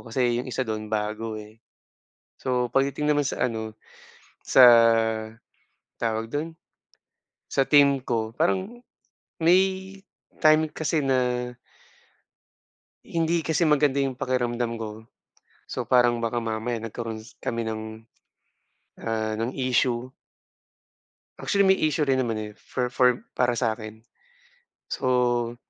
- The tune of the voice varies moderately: Yes, average, 4.2 semitones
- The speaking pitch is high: No, low, 125 Hz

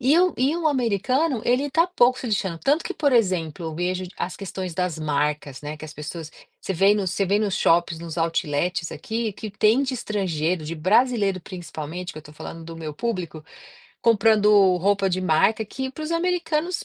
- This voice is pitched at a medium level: No, high, 195 Hz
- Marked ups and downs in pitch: Yes, wide, 6.5 semitones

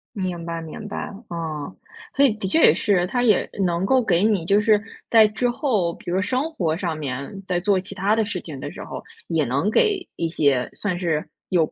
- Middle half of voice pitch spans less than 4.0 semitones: No, average, 4.3 semitones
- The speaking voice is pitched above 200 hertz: No, medium, 185 Hz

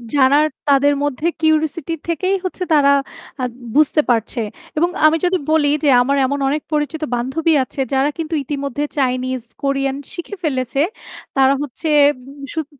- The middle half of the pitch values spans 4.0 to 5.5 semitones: No, average, 2.8 semitones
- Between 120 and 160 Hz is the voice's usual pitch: No, very high, 285 Hz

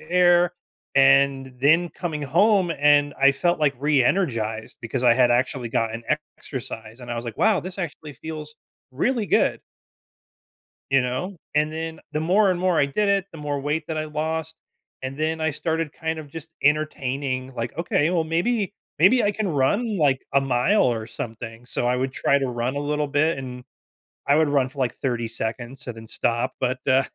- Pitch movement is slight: No, average, 4.2 semitones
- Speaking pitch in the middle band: Yes, medium, 145 Hz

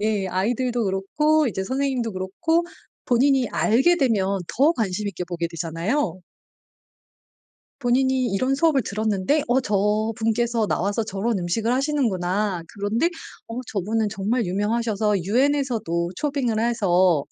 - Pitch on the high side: Yes, high, 220 Hz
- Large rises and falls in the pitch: No, average, 4.9 semitones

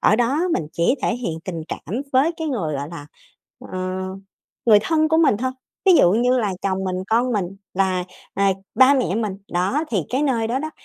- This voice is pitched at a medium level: No, high, 225 Hz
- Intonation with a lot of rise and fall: Yes, wide, 5.8 semitones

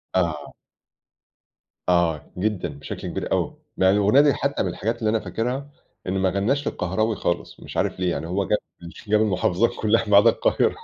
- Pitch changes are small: No, average, 3.8 semitones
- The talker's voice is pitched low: Yes, low, 100 Hz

